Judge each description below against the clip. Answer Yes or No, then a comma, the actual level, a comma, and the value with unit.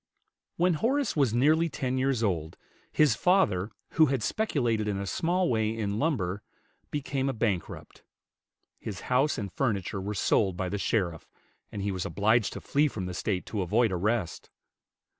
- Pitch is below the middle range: Yes, low, 110 Hz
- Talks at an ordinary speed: Yes, average, 165 wpm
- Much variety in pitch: Yes, wide, 6.2 semitones